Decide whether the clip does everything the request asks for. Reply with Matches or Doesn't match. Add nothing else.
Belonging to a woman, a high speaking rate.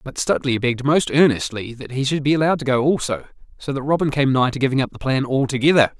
Doesn't match